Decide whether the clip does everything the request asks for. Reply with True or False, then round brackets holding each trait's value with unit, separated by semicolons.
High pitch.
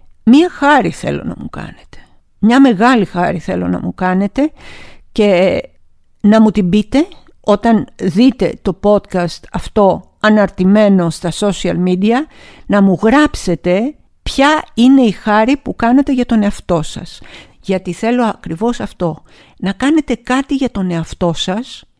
True (210 Hz)